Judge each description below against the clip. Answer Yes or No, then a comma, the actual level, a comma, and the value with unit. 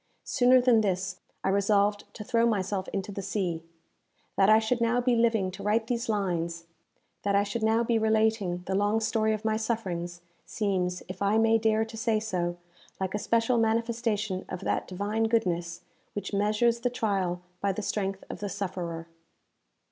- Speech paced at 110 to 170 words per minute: No, average, 180 wpm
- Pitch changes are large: No, average, 2.9 semitones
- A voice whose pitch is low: No, high, 210 Hz